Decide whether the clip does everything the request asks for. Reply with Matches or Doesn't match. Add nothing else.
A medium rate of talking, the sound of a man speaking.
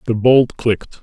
Matches